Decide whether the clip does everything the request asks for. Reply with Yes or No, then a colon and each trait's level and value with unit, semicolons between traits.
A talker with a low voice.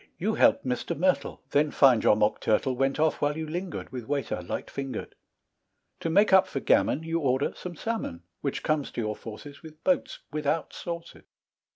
No: medium, 145 Hz